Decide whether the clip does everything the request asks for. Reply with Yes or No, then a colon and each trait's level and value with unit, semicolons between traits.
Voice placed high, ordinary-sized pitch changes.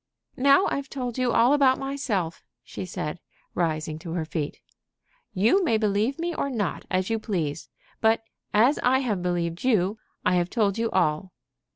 No: high, 210 Hz; wide, 6.5 semitones